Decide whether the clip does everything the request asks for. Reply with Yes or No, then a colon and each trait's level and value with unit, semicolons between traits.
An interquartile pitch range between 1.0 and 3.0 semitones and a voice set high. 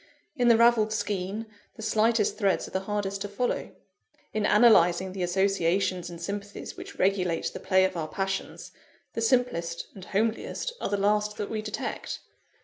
Yes: narrow, 2.5 semitones; high, 200 Hz